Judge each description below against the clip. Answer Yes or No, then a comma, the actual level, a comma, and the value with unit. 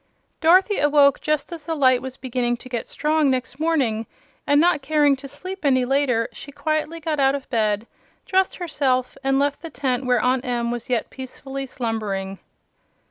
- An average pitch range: Yes, average, 3.4 semitones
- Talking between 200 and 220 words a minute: No, average, 180 wpm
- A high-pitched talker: Yes, very high, 270 Hz